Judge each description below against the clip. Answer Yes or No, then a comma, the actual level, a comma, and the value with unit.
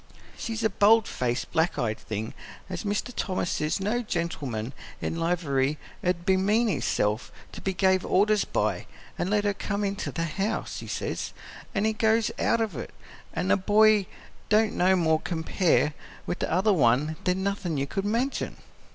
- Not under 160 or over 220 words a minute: Yes, average, 170 wpm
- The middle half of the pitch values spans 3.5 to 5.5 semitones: Yes, average, 4.7 semitones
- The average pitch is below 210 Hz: Yes, high, 190 Hz